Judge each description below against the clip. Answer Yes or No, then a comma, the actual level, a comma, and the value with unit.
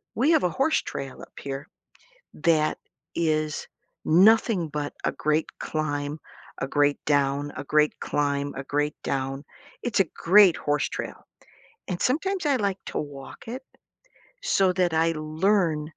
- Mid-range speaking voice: Yes, medium, 155 Hz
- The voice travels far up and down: No, average, 4.9 semitones